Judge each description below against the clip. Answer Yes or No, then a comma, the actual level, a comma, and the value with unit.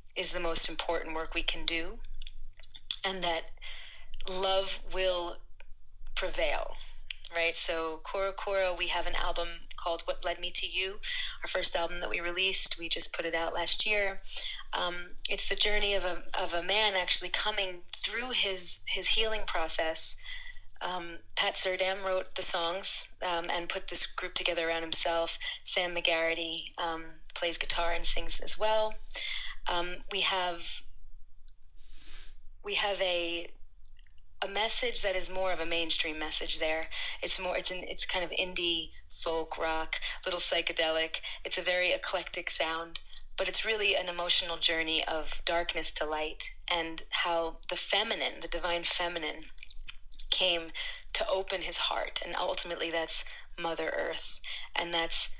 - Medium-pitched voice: Yes, medium, 175 Hz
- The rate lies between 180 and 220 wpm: No, average, 155 wpm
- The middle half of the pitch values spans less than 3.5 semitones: Yes, narrow, 2.5 semitones